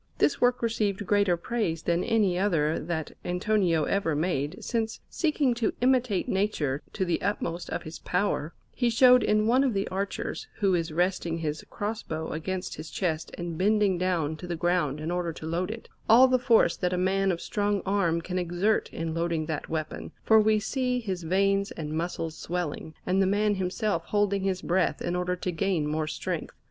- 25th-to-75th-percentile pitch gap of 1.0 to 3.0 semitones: No, average, 4.0 semitones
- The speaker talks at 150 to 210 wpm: Yes, average, 195 wpm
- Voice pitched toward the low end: No, medium, 185 Hz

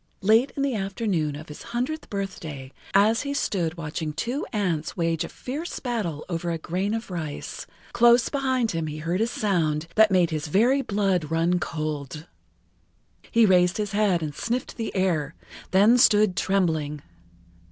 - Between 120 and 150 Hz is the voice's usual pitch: No, high, 190 Hz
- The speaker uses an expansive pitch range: Yes, wide, 5.8 semitones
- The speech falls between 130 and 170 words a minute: Yes, average, 165 wpm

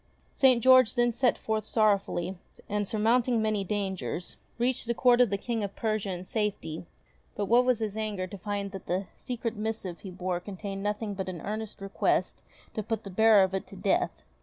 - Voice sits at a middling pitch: No, high, 210 Hz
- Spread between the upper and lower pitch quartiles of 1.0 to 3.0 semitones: Yes, narrow, 2.6 semitones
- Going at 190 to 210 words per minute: Yes, average, 195 wpm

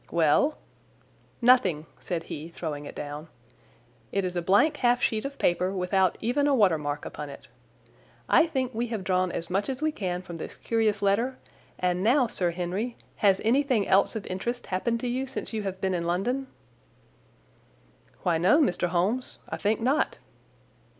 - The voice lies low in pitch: No, high, 195 Hz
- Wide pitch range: Yes, wide, 5.7 semitones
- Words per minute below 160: No, average, 175 wpm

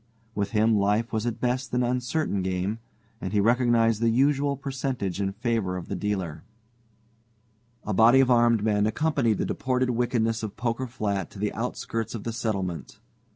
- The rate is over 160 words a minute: Yes, average, 170 wpm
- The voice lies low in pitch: Yes, low, 115 Hz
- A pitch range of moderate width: Yes, average, 3.2 semitones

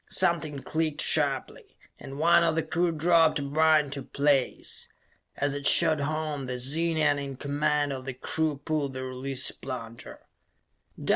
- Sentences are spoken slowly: No, average, 150 wpm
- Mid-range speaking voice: Yes, medium, 145 Hz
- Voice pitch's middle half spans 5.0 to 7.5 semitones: No, narrow, 2.4 semitones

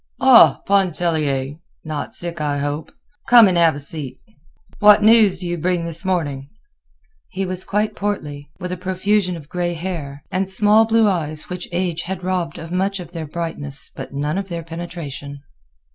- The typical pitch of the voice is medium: Yes, medium, 175 Hz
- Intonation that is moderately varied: Yes, average, 3.8 semitones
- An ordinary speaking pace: Yes, average, 175 wpm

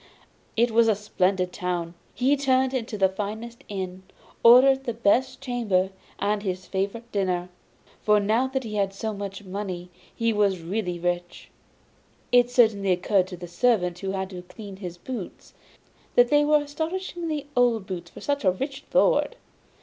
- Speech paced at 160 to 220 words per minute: Yes, average, 165 wpm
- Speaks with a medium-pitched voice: No, high, 210 Hz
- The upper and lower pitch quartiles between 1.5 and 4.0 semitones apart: No, average, 4.9 semitones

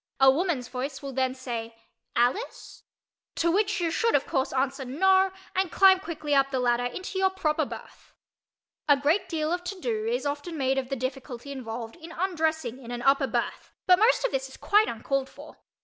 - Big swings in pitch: Yes, wide, 6.0 semitones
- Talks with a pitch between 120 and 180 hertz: No, very high, 285 Hz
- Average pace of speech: Yes, average, 195 wpm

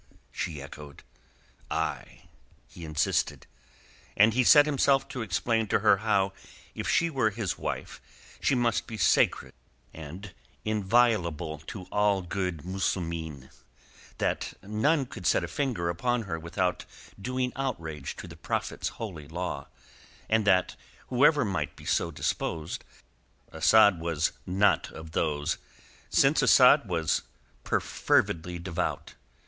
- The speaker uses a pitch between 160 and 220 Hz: No, very low, 95 Hz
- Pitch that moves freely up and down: Yes, wide, 5.8 semitones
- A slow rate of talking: Yes, slow, 125 wpm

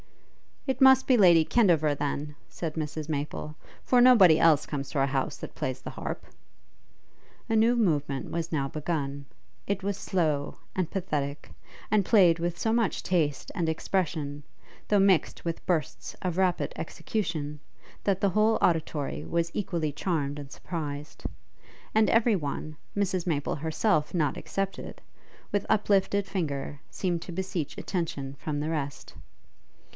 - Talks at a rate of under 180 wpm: Yes, average, 145 wpm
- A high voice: No, medium, 165 Hz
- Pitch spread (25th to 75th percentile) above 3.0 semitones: Yes, average, 4.7 semitones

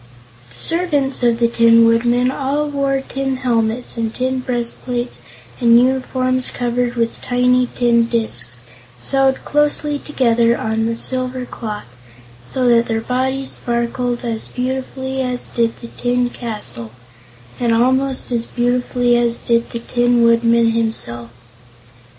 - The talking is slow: Yes, slow, 130 wpm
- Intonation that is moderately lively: No, narrow, 1.8 semitones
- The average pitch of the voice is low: No, high, 245 Hz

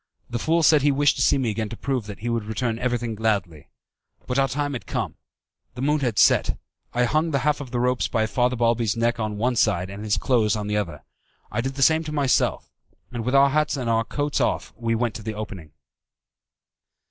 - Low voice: Yes, low, 120 Hz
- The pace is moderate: No, fast, 230 wpm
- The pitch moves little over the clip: No, average, 3.9 semitones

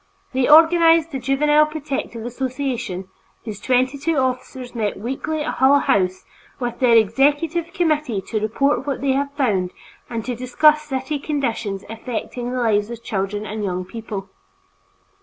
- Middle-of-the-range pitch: No, very high, 255 Hz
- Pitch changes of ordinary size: Yes, average, 4.8 semitones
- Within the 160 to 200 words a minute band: No, average, 150 wpm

